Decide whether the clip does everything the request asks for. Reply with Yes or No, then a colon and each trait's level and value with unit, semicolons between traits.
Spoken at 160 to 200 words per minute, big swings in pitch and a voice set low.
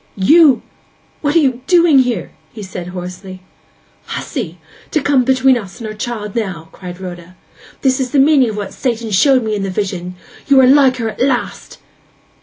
No: average, 190 wpm; wide, 5.9 semitones; high, 230 Hz